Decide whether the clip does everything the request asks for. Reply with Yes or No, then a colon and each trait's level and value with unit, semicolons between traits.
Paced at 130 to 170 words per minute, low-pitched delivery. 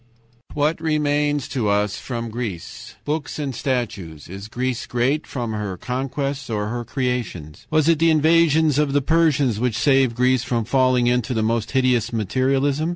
Yes: average, 160 wpm; low, 130 Hz